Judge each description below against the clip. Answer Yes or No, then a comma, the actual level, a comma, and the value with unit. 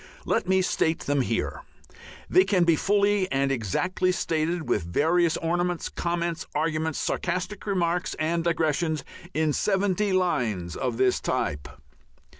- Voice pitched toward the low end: No, medium, 170 Hz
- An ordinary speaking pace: No, slow, 130 wpm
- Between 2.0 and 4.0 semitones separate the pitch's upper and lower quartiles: Yes, average, 3.4 semitones